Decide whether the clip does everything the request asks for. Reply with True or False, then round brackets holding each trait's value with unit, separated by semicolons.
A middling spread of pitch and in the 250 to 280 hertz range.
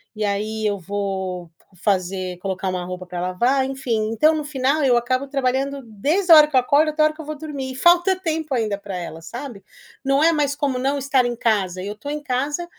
False (6.5 semitones; 255 Hz)